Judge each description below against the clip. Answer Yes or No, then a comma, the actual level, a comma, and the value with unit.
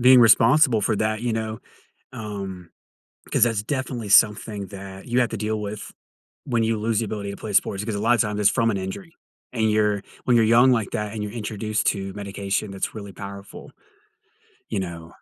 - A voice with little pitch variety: Yes, narrow, 2.3 semitones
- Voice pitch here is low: Yes, low, 105 Hz